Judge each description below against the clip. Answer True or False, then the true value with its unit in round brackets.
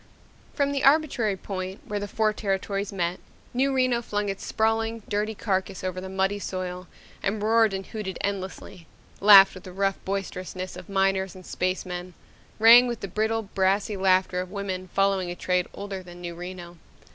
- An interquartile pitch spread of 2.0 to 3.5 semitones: True (2.4 semitones)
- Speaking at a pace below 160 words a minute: False (170 wpm)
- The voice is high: True (195 Hz)